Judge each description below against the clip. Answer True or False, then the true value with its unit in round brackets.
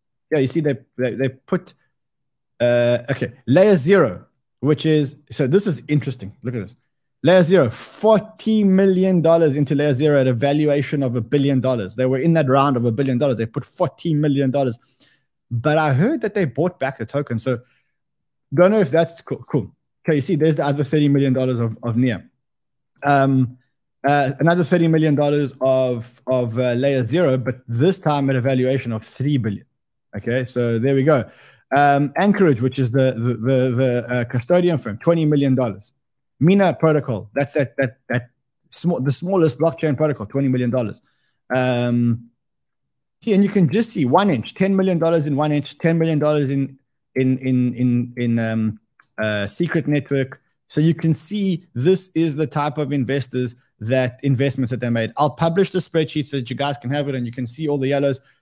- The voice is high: False (140 Hz)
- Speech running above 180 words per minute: True (190 wpm)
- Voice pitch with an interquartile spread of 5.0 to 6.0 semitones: False (3.8 semitones)